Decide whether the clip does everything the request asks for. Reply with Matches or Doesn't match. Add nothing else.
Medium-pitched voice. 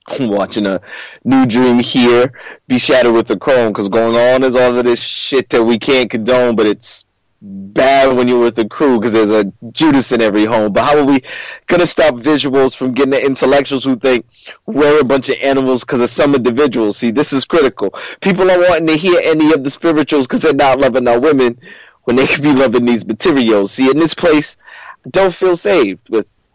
Doesn't match